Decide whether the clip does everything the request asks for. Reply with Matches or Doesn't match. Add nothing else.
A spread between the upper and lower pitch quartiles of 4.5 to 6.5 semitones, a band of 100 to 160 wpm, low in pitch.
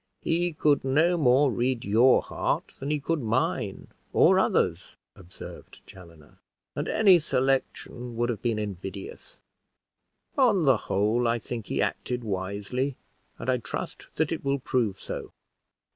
Matches